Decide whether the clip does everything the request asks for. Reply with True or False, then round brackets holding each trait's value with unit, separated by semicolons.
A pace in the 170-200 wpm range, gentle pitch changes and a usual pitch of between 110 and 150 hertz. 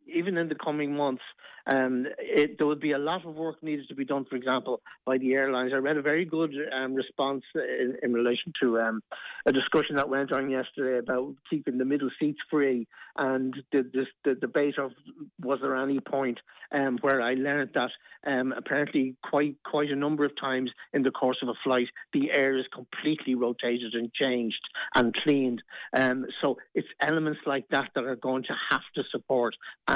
True (195 wpm; 2.3 semitones; 135 Hz)